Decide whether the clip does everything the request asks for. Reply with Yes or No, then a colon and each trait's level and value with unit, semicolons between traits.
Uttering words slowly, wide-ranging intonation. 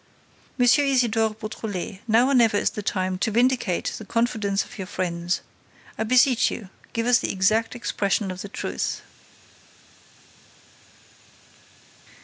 No: slow, 130 wpm; average, 3.5 semitones